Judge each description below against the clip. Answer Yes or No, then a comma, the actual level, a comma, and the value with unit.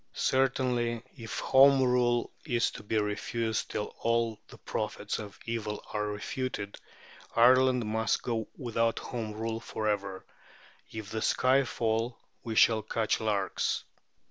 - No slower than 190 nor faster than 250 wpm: No, slow, 135 wpm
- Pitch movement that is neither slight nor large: No, narrow, 2.3 semitones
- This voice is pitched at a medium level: No, low, 115 Hz